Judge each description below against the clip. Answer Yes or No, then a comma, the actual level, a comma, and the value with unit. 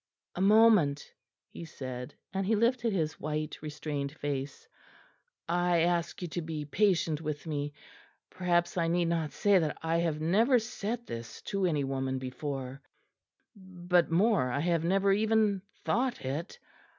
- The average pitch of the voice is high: No, medium, 170 Hz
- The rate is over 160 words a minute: No, average, 150 wpm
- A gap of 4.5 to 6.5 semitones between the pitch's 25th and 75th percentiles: Yes, average, 4.8 semitones